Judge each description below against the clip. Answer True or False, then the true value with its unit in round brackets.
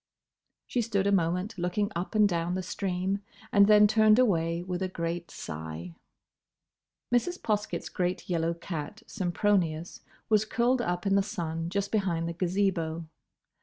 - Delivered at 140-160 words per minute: True (150 wpm)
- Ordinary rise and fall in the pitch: True (3.5 semitones)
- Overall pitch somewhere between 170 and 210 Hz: True (185 Hz)